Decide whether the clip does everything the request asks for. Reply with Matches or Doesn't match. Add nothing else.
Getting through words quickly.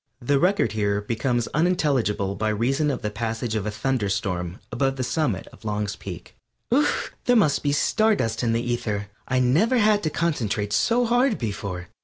Doesn't match